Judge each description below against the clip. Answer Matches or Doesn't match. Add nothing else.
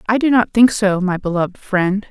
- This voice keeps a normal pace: Doesn't match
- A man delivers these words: Doesn't match